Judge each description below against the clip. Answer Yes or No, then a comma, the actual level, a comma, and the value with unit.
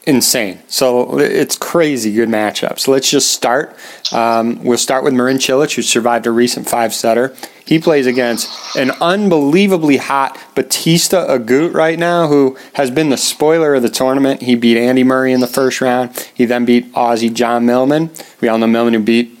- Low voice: Yes, low, 130 Hz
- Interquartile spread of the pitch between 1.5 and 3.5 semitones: Yes, average, 3.0 semitones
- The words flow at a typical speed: Yes, average, 180 wpm